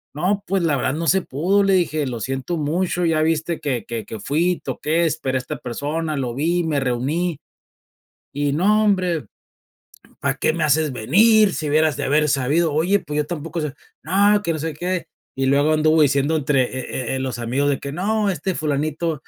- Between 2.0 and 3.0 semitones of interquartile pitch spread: No, average, 3.6 semitones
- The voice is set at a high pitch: No, medium, 155 Hz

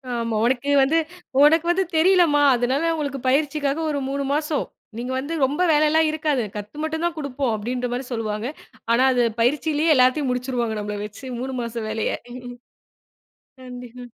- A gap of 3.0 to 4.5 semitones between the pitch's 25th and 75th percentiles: Yes, average, 3.8 semitones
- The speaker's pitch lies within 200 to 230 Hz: No, very high, 270 Hz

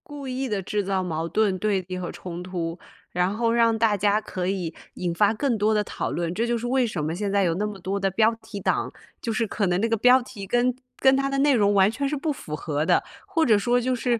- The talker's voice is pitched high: Yes, high, 210 Hz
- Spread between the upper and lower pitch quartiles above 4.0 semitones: Yes, average, 4.6 semitones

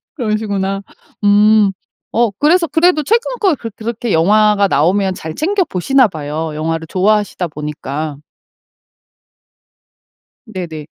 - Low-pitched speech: No, high, 205 Hz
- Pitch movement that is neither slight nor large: No, wide, 6.5 semitones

